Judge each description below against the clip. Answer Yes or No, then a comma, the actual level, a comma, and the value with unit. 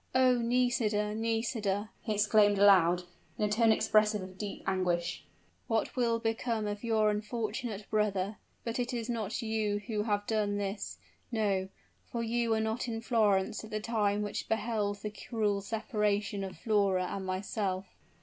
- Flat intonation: Yes, narrow, 1.9 semitones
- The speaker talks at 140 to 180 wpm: Yes, average, 160 wpm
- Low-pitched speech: No, high, 210 Hz